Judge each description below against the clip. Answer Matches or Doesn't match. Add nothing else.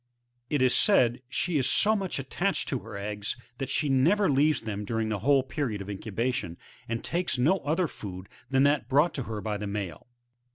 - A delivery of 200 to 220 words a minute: Matches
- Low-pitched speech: Matches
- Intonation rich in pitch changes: Matches